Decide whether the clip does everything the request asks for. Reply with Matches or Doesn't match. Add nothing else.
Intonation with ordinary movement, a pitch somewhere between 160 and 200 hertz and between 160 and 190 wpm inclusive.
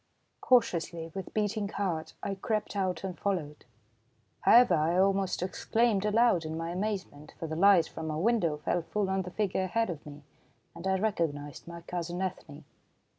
Matches